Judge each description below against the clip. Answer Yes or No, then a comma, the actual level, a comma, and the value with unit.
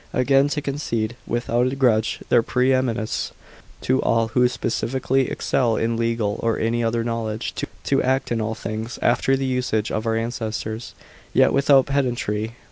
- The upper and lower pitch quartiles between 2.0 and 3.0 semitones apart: Yes, narrow, 2.6 semitones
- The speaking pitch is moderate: No, low, 120 Hz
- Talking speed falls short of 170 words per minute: Yes, average, 160 wpm